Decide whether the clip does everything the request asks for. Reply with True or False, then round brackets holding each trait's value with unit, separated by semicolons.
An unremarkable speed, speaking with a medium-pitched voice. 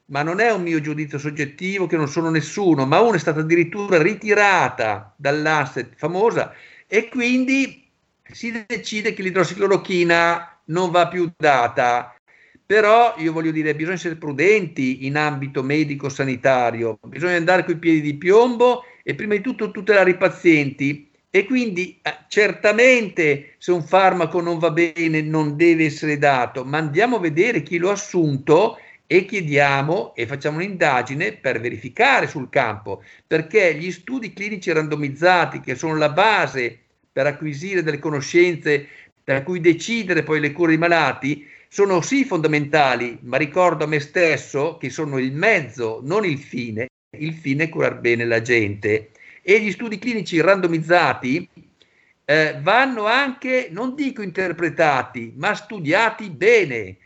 True (145 wpm; 165 Hz)